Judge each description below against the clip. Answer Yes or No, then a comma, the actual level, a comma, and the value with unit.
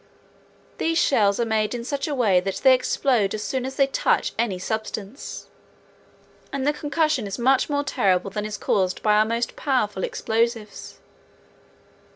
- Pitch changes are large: No, average, 4.4 semitones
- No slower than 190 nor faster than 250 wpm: No, average, 165 wpm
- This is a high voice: Yes, high, 230 Hz